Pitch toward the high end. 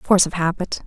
No: medium, 175 Hz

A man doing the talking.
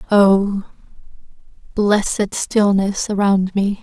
No: female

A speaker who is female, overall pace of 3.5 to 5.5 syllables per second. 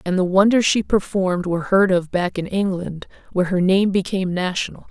No: female; 5.7 syllables/s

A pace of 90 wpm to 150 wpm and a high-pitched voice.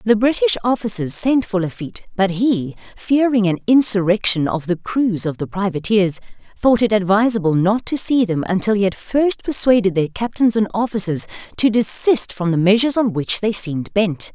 No: average, 180 wpm; high, 205 Hz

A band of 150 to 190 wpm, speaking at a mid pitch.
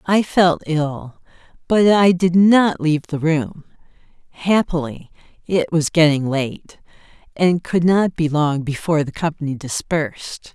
No: slow, 135 wpm; medium, 160 Hz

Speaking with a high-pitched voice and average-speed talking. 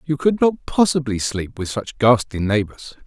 No: low, 125 Hz; average, 175 wpm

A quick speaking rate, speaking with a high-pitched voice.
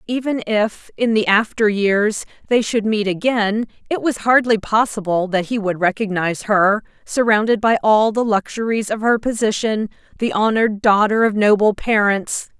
No: average, 155 wpm; high, 215 Hz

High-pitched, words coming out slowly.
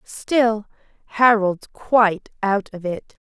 Yes: high, 215 Hz; slow, 110 wpm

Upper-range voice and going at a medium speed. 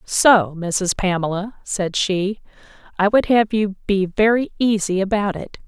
Yes: high, 200 Hz; average, 150 wpm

